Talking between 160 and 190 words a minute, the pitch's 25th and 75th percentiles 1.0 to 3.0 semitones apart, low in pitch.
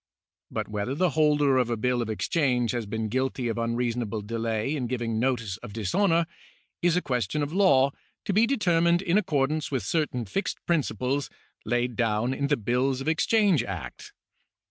No: average, 175 wpm; average, 5.2 semitones; low, 130 Hz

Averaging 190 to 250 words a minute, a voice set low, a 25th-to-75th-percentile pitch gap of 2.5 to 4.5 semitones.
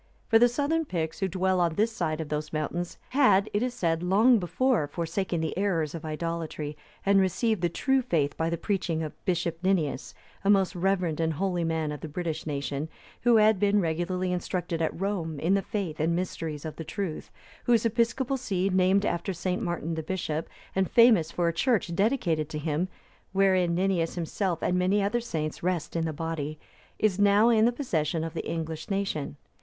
No: average, 195 wpm; medium, 180 Hz; average, 3.8 semitones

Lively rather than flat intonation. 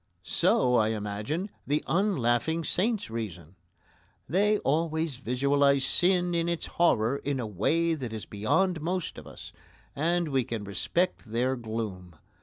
Yes: wide, 7.2 semitones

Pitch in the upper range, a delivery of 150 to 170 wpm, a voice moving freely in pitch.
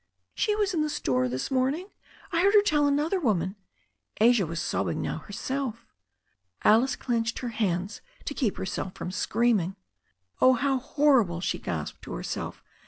Yes: high, 235 Hz; average, 165 wpm; wide, 7.2 semitones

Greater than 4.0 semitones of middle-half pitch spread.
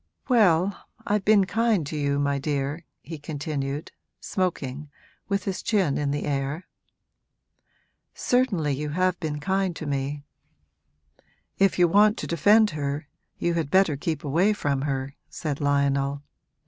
Yes: average, 5.0 semitones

